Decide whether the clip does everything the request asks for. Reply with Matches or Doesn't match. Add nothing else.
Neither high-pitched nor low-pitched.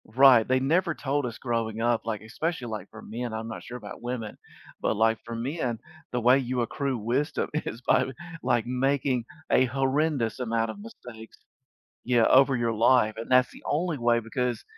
Doesn't match